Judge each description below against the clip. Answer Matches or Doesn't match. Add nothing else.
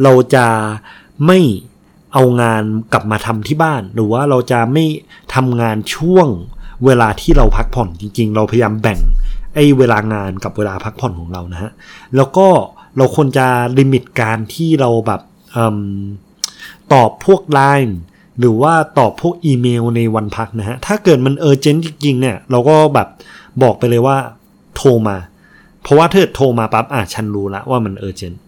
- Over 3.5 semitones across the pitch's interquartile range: Matches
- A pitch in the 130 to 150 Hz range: Doesn't match